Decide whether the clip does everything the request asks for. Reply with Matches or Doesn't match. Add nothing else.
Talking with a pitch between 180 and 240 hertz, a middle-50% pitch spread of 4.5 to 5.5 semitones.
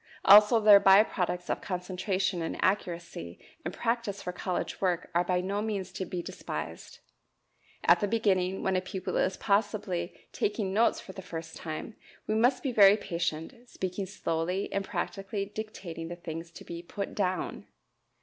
Doesn't match